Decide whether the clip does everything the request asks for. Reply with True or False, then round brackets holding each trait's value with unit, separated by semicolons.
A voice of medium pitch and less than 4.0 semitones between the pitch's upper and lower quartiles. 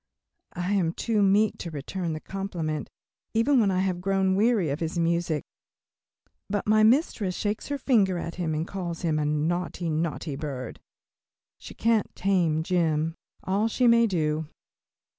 False (180 Hz; 4.3 semitones)